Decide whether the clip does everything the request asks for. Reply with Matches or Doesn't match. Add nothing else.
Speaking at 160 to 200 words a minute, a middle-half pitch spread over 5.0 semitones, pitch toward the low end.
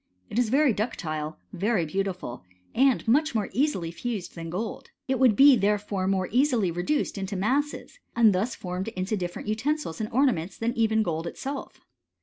Doesn't match